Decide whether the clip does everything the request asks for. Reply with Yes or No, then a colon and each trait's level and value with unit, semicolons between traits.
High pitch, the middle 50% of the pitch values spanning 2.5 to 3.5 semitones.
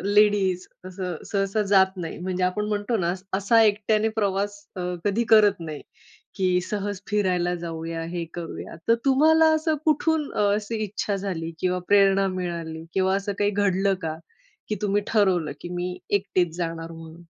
Yes: high, 195 Hz; average, 2.8 semitones